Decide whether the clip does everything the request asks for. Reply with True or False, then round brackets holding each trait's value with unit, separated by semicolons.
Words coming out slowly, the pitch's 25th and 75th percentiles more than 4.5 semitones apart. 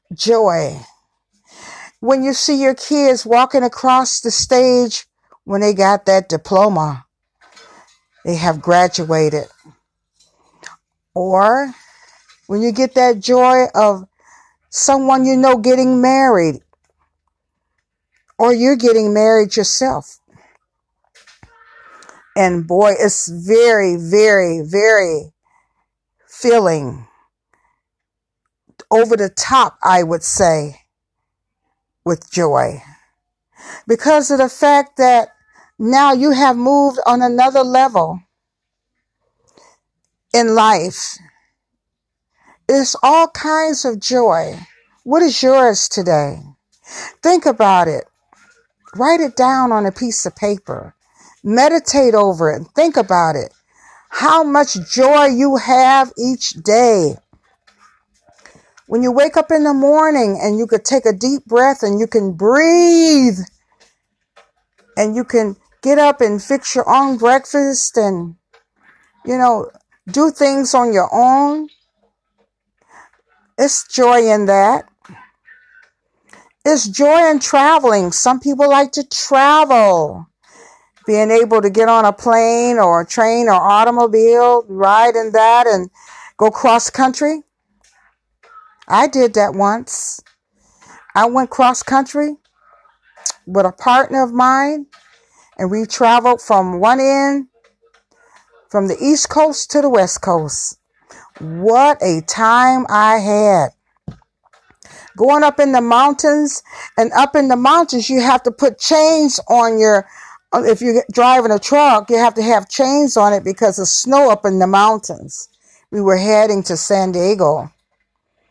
True (120 wpm; 5.1 semitones)